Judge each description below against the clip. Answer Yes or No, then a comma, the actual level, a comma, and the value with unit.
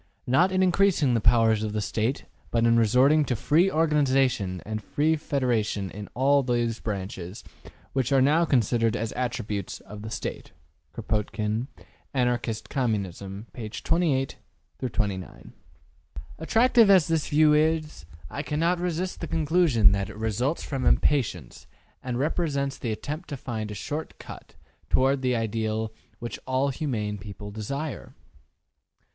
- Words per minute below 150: Yes, average, 140 wpm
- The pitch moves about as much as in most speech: No, wide, 5.7 semitones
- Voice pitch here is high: No, low, 125 Hz